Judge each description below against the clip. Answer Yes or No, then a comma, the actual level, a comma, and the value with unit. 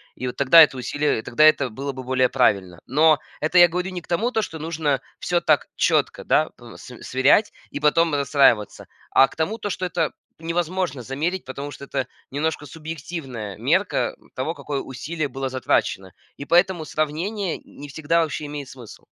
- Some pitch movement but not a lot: Yes, average, 3.9 semitones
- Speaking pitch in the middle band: Yes, medium, 150 Hz